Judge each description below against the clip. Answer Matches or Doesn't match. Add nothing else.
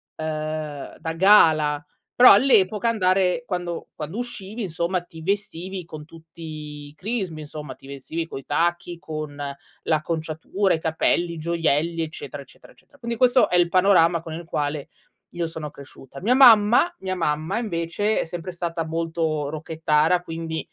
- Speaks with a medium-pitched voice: Matches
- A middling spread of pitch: Matches